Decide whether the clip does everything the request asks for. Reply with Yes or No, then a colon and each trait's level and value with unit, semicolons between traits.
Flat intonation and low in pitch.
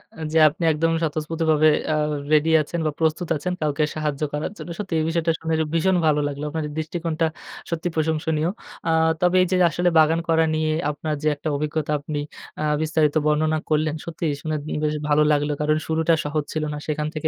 No: narrow, 1.3 semitones; medium, 155 Hz